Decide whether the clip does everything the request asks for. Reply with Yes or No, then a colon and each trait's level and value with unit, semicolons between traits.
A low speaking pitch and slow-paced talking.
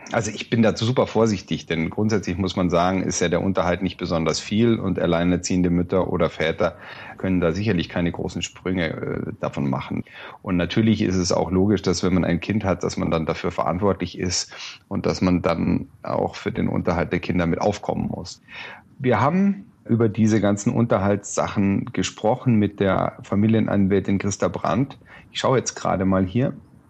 No: very low, 95 Hz; average, 180 wpm